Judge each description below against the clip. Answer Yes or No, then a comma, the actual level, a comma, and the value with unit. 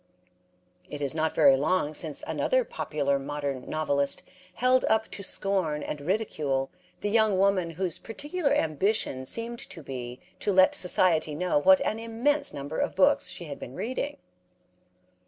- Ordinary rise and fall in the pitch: No, wide, 7.0 semitones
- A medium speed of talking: Yes, average, 155 wpm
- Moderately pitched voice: Yes, medium, 175 Hz